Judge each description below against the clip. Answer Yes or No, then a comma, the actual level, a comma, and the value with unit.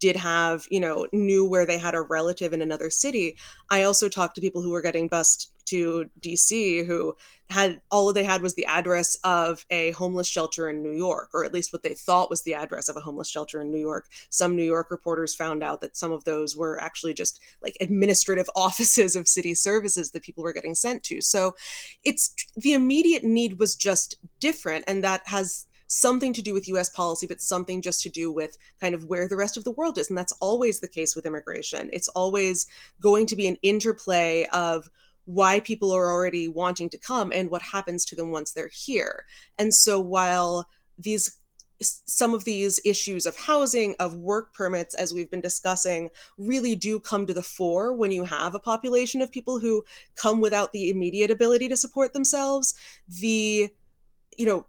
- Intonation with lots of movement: No, average, 3.8 semitones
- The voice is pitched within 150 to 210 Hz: Yes, medium, 185 Hz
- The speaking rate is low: No, average, 200 wpm